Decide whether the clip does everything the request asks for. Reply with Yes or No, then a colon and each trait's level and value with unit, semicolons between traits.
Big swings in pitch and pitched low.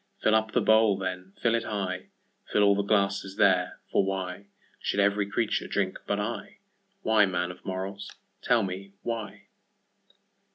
No: narrow, 2.4 semitones; low, 100 Hz